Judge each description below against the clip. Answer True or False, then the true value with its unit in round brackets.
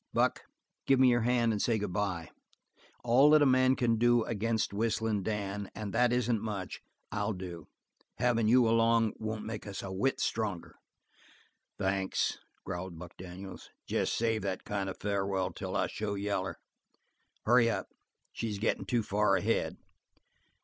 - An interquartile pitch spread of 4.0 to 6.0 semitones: False (3.0 semitones)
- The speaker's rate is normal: True (155 wpm)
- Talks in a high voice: False (110 Hz)